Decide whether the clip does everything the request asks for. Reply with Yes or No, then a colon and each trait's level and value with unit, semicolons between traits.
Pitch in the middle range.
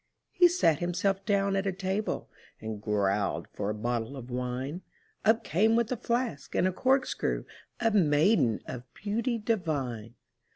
Yes: medium, 180 Hz